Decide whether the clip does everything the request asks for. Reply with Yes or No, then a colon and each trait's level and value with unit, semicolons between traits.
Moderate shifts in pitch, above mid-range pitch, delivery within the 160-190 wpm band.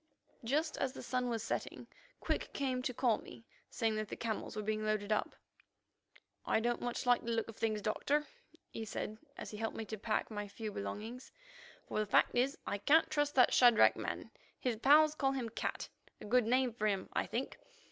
No: average, 3.0 semitones; high, 230 Hz; fast, 205 wpm